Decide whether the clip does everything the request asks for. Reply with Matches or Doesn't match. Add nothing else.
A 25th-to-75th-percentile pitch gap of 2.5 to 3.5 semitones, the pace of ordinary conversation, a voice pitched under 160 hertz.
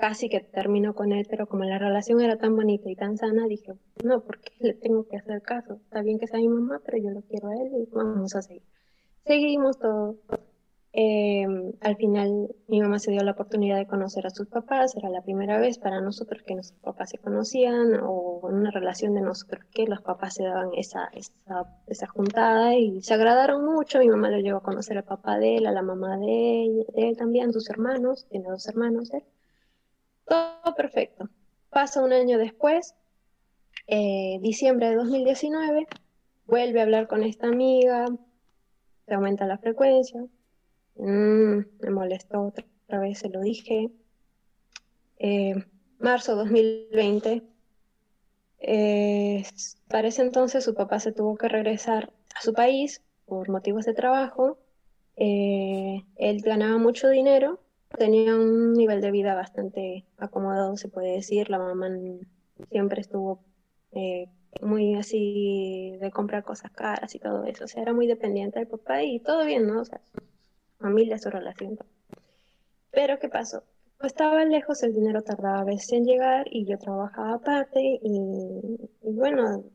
Doesn't match